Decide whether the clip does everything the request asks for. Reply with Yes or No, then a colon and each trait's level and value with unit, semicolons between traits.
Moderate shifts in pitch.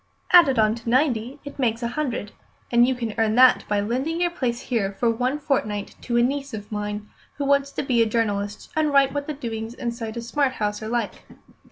Yes: average, 3.9 semitones